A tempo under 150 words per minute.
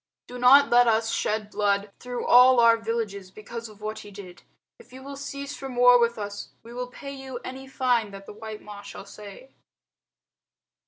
No: average, 200 wpm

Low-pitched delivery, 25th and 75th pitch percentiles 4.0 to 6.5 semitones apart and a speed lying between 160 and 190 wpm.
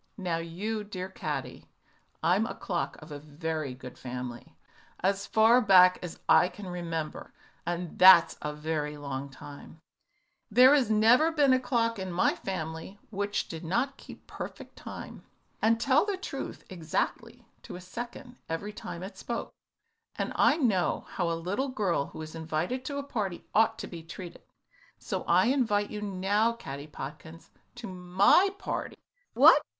No: medium, 185 Hz; wide, 5.6 semitones; average, 165 wpm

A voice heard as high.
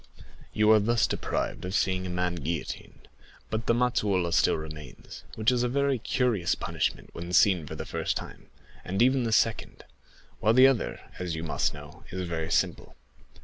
No: very low, 95 Hz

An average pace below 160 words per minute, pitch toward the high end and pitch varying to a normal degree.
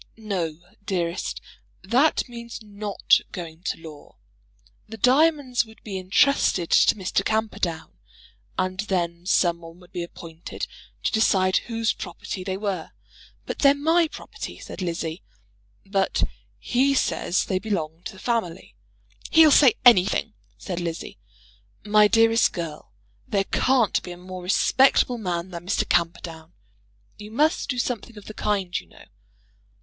Yes: average, 140 wpm; high, 195 Hz; average, 4.6 semitones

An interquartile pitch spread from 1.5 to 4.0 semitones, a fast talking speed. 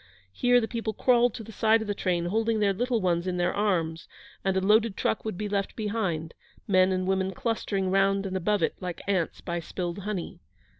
Yes: average, 3.1 semitones; fast, 210 wpm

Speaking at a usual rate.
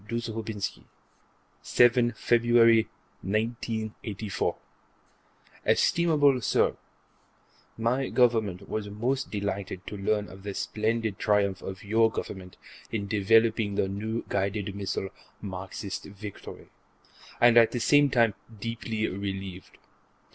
No: slow, 105 wpm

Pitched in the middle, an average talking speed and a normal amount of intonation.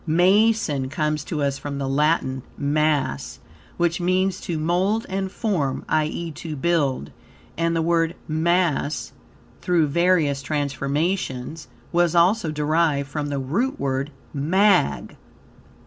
No: medium, 155 Hz; slow, 120 wpm; average, 3.7 semitones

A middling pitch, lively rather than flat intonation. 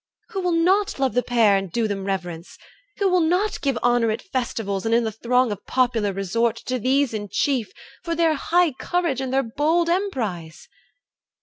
No: very high, 250 Hz; wide, 7.5 semitones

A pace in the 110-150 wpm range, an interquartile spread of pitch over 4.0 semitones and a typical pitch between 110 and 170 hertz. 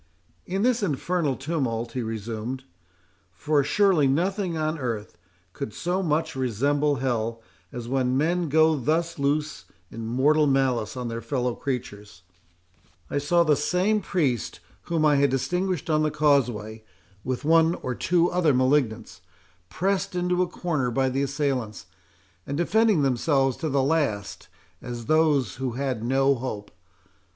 Yes: average, 140 wpm; average, 5.1 semitones; medium, 140 Hz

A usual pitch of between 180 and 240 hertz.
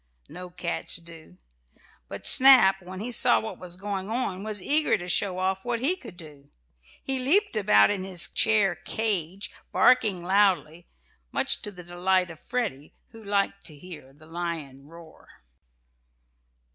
Yes: medium, 185 Hz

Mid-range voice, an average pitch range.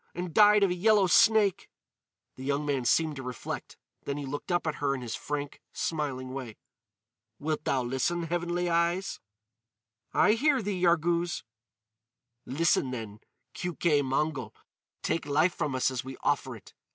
Yes: medium, 155 Hz; average, 4.7 semitones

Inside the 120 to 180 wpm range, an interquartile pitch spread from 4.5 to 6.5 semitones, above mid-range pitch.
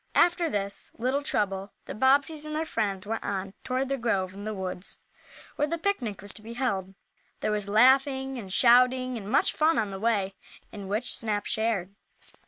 No: average, 190 wpm; average, 5.0 semitones; high, 225 Hz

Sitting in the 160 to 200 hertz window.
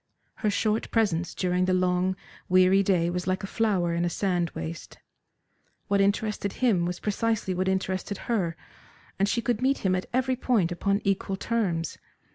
Yes: high, 190 Hz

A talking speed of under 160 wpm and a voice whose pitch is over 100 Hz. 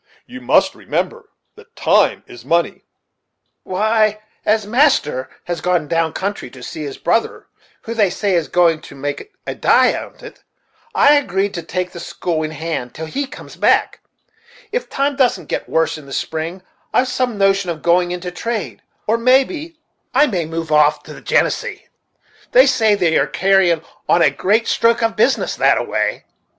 No: average, 175 wpm; high, 190 Hz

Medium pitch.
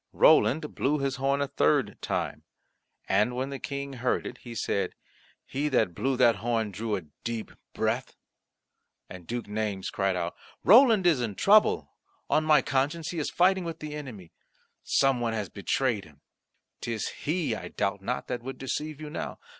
No: low, 130 Hz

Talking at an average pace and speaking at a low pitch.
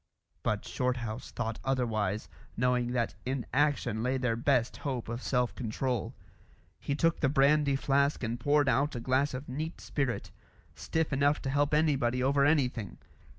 Yes: average, 155 wpm; low, 130 Hz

